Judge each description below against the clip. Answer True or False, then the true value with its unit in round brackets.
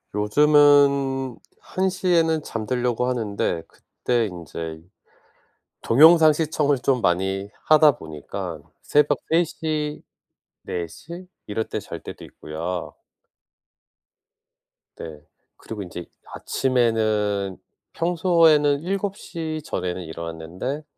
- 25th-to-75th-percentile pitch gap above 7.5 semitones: True (8.0 semitones)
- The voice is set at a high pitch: False (125 Hz)